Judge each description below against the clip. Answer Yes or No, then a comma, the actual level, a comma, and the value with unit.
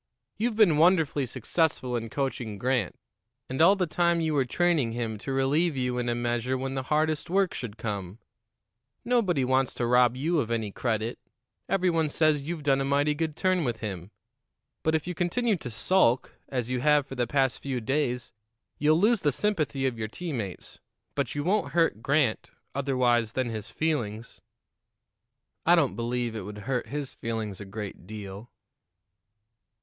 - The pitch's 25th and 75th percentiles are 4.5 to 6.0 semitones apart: Yes, average, 5.2 semitones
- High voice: No, low, 135 Hz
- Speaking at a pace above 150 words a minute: Yes, average, 175 wpm